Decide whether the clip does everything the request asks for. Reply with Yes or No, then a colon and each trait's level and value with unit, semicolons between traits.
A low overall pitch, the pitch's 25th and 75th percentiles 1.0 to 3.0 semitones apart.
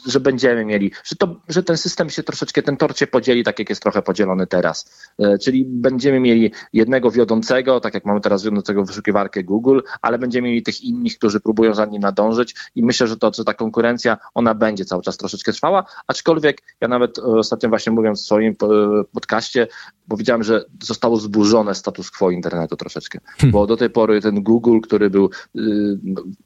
No: low, 110 Hz; average, 3.6 semitones